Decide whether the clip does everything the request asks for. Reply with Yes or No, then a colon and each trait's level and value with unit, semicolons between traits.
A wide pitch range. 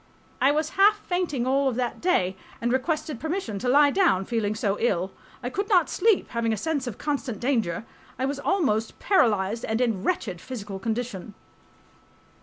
Yes: wide, 5.9 semitones